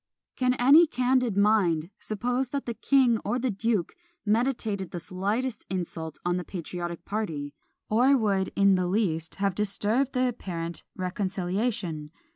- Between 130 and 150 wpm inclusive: Yes, average, 140 wpm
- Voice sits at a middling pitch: No, high, 205 Hz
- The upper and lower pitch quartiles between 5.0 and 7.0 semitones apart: Yes, wide, 5.4 semitones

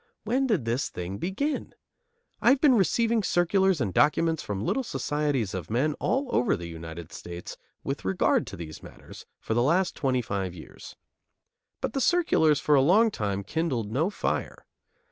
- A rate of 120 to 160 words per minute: No, average, 170 wpm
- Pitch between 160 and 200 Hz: No, medium, 145 Hz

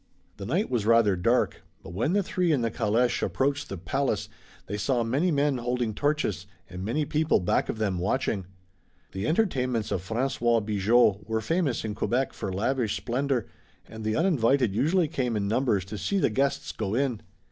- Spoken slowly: No, average, 180 wpm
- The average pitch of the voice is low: Yes, low, 120 Hz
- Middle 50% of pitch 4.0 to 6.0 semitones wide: Yes, average, 5.0 semitones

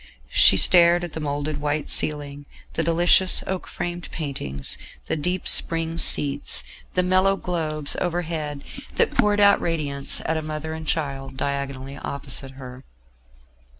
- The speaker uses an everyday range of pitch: Yes, average, 3.5 semitones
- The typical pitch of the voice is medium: Yes, medium, 155 Hz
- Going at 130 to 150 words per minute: Yes, average, 140 wpm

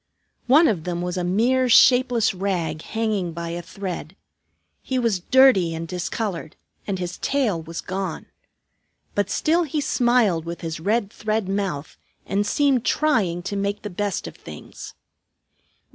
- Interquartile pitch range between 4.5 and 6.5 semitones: Yes, average, 5.2 semitones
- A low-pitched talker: No, high, 195 Hz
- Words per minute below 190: Yes, average, 150 wpm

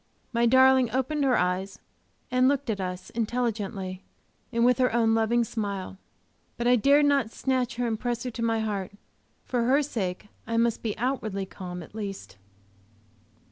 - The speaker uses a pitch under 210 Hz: No, high, 230 Hz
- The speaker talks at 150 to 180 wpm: Yes, average, 170 wpm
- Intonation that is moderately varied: Yes, average, 3.8 semitones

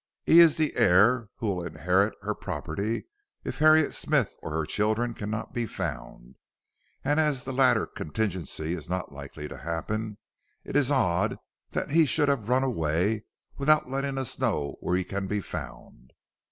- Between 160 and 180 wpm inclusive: Yes, average, 165 wpm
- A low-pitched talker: Yes, low, 105 Hz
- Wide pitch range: Yes, wide, 7.1 semitones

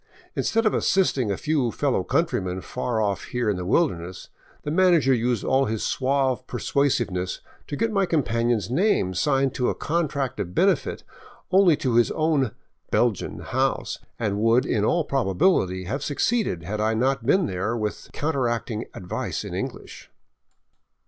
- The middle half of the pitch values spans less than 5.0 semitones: No, wide, 5.6 semitones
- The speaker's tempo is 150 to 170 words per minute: Yes, average, 155 wpm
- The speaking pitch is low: Yes, low, 125 Hz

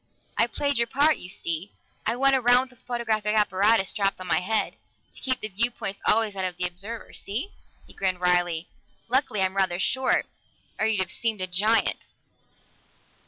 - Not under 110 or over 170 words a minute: No, average, 180 wpm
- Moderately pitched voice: No, high, 210 Hz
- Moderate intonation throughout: Yes, average, 4.2 semitones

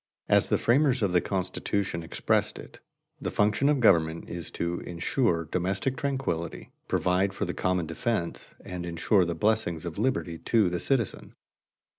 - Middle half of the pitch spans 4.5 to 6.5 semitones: Yes, average, 4.8 semitones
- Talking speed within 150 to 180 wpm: Yes, average, 155 wpm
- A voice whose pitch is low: Yes, very low, 90 Hz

